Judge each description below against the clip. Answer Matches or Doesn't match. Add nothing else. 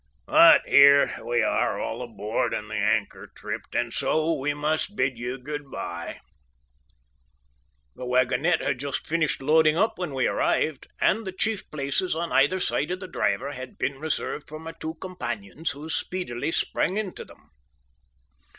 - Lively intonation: Doesn't match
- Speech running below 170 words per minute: Matches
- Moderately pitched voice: Matches